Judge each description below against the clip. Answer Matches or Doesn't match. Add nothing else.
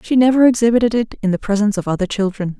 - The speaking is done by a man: Doesn't match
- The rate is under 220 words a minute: Doesn't match